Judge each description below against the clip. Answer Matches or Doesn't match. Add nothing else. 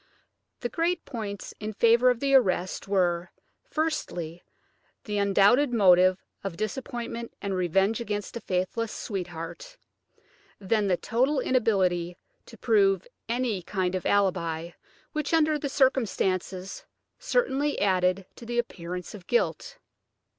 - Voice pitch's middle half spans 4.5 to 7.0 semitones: Matches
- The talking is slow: Matches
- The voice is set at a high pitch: Matches